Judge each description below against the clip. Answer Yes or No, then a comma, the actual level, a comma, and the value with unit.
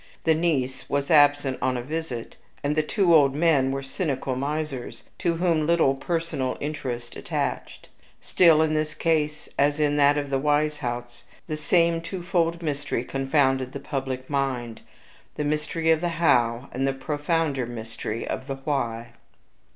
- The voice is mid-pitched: Yes, medium, 145 Hz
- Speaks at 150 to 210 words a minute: Yes, average, 155 wpm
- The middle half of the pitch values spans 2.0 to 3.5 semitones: Yes, average, 3.2 semitones